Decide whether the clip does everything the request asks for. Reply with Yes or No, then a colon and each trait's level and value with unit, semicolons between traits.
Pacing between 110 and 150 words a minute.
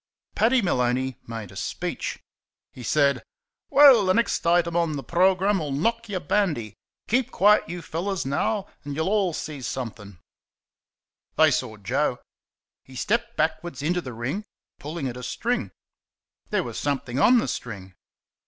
Yes: average, 145 wpm